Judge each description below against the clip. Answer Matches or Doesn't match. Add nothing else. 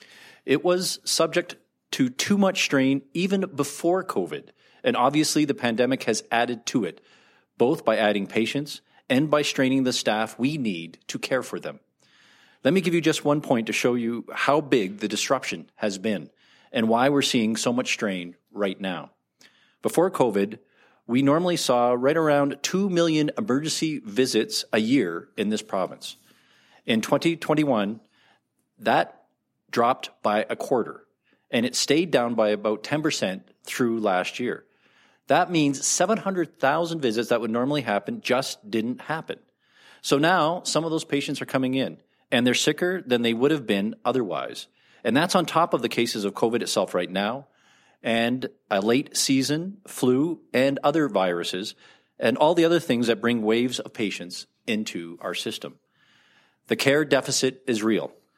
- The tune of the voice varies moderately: Doesn't match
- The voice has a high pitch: Doesn't match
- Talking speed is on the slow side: Doesn't match